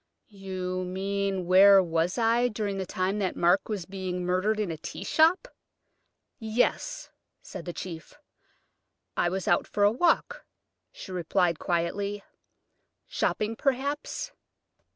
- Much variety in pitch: No, average, 3.2 semitones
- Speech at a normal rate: No, slow, 130 wpm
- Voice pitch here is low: No, high, 195 Hz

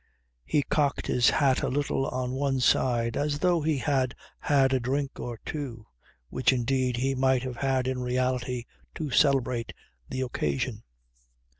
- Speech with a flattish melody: Yes, narrow, 1.8 semitones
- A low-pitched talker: Yes, low, 130 Hz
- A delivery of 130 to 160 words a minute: Yes, average, 155 wpm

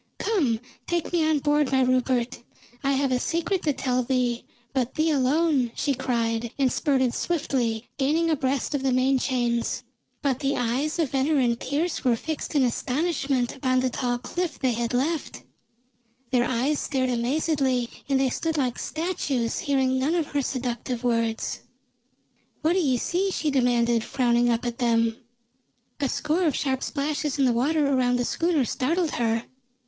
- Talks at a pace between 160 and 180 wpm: Yes, average, 170 wpm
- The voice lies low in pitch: No, very high, 265 Hz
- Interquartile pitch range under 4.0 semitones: Yes, average, 3.5 semitones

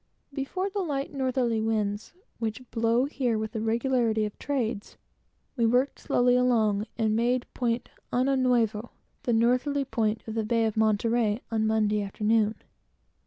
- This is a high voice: Yes, high, 230 Hz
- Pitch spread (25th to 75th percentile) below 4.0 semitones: Yes, narrow, 2.6 semitones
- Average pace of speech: Yes, average, 150 wpm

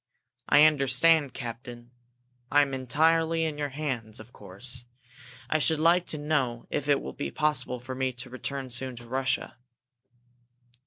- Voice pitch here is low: Yes, low, 130 Hz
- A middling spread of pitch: Yes, average, 3.7 semitones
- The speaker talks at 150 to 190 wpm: Yes, average, 155 wpm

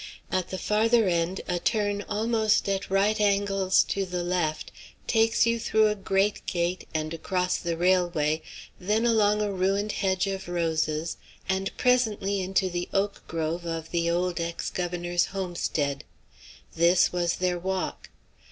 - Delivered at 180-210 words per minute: No, average, 150 wpm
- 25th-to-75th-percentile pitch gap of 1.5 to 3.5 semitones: Yes, average, 2.8 semitones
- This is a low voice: No, medium, 185 Hz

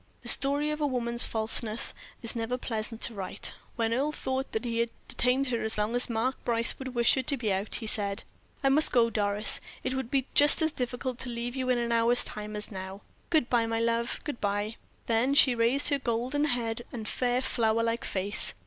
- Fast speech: Yes, fast, 215 wpm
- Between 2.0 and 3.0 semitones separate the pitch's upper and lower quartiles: Yes, narrow, 2.5 semitones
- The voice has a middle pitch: No, high, 235 Hz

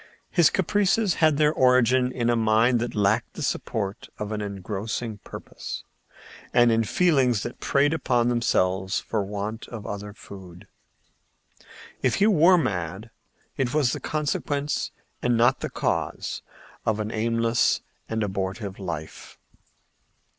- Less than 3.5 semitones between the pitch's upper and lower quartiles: No, average, 4.6 semitones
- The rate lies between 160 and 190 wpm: No, slow, 135 wpm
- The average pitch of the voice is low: Yes, low, 115 Hz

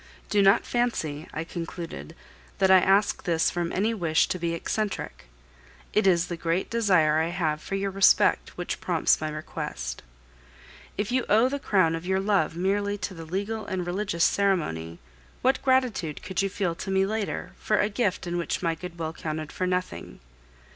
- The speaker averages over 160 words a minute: Yes, average, 180 wpm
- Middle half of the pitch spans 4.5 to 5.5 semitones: No, average, 3.5 semitones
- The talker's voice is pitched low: No, medium, 185 Hz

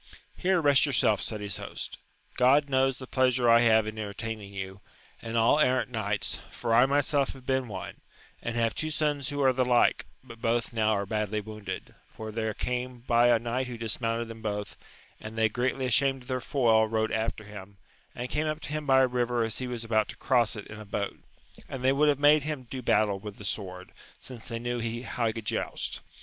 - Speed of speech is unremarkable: No, fast, 220 wpm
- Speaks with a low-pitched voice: Yes, low, 120 Hz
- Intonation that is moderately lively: Yes, average, 3.1 semitones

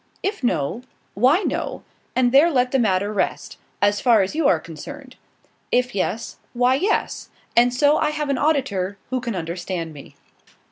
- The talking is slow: No, average, 170 wpm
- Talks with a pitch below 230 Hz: No, high, 245 Hz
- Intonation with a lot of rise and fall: Yes, wide, 6.3 semitones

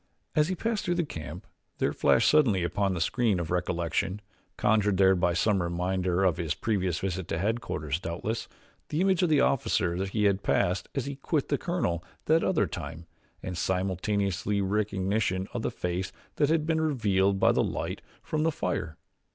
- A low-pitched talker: Yes, low, 100 Hz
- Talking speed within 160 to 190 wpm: Yes, average, 180 wpm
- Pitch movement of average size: No, wide, 6.5 semitones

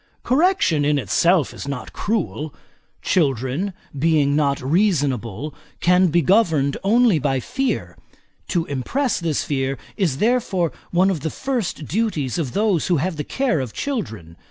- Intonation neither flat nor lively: No, wide, 6.4 semitones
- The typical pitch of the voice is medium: Yes, medium, 165 Hz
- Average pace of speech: Yes, average, 145 wpm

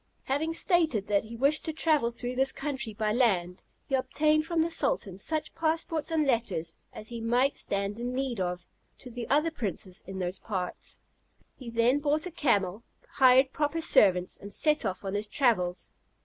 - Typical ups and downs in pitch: No, wide, 6.8 semitones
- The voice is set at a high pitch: Yes, high, 245 Hz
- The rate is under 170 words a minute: No, average, 180 wpm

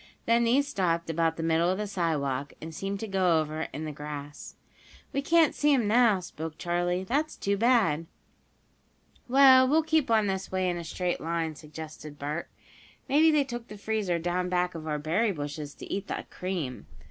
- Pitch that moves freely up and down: Yes, wide, 6.2 semitones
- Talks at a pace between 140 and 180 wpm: No, average, 190 wpm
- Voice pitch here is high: No, medium, 180 Hz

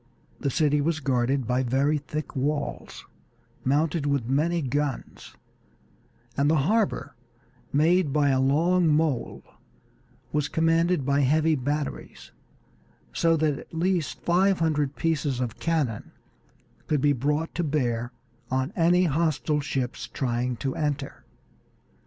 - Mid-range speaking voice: Yes, medium, 150 Hz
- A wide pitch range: No, average, 3.2 semitones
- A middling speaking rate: No, slow, 125 wpm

